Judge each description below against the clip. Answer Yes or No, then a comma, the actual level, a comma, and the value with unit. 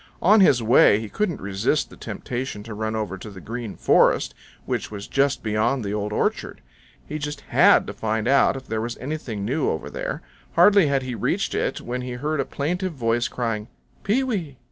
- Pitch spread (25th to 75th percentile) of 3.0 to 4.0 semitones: No, average, 5.2 semitones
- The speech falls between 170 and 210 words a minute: Yes, average, 200 wpm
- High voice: No, low, 120 Hz